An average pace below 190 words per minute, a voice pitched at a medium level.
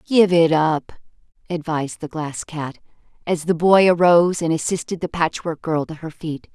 Yes: average, 175 wpm; medium, 165 Hz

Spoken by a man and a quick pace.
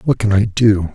Yes: male; fast, 255 wpm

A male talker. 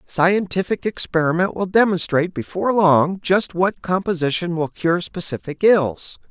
Yes: male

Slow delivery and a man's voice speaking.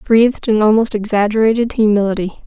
No: slow, 120 wpm; female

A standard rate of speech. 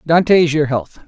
Yes: average, 170 wpm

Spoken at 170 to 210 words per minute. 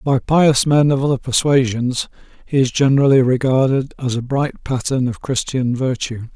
No: average, 160 wpm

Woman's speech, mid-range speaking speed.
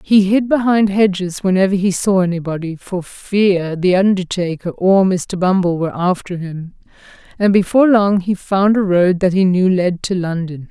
Yes: female; average, 175 wpm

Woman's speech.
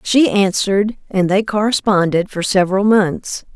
Yes: female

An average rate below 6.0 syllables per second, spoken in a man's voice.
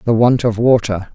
Yes: 5.0 syllables/s; male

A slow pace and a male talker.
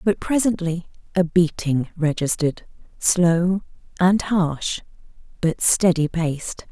No: slow, 100 wpm; female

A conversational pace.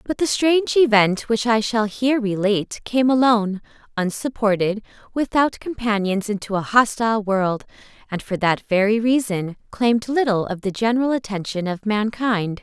Yes: average, 145 wpm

